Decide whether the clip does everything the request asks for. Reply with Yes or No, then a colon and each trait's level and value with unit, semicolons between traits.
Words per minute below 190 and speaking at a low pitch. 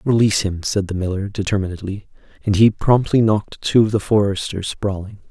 Yes: average, 170 wpm; low, 100 Hz